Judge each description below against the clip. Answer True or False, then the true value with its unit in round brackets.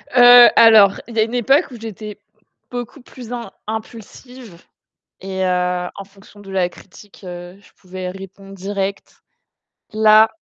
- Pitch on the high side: True (205 Hz)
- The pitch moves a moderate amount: True (3.2 semitones)